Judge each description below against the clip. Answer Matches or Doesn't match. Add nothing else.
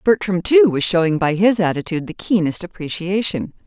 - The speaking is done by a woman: Matches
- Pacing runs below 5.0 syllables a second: Doesn't match